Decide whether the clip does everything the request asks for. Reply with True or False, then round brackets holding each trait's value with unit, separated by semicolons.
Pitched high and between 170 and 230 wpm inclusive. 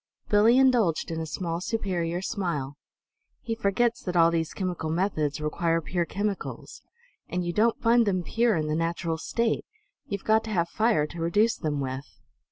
False (175 Hz; 175 wpm)